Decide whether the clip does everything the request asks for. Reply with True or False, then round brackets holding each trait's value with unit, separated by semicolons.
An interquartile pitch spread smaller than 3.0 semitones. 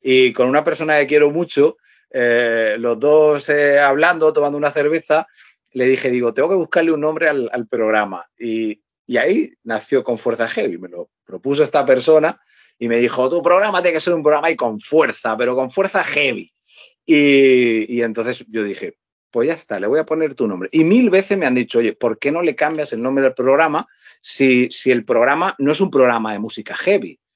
False (4.6 semitones)